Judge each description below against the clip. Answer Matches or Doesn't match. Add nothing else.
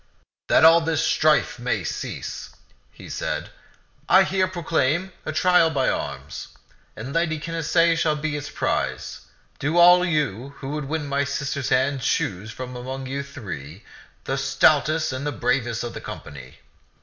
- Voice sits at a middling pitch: Matches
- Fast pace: Doesn't match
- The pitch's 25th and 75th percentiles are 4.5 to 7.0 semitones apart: Doesn't match